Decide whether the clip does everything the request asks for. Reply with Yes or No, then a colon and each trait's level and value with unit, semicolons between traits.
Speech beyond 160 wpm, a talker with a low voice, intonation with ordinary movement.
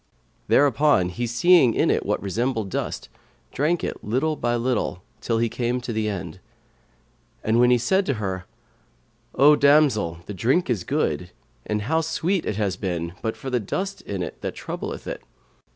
No: average, 170 wpm; low, 120 Hz; wide, 5.8 semitones